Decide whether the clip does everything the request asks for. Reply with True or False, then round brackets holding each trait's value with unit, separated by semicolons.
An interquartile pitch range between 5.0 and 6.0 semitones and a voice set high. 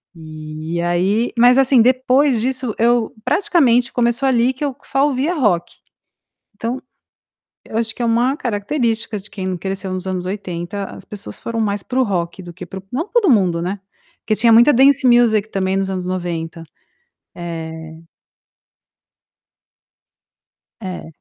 True (5.6 semitones; 220 Hz)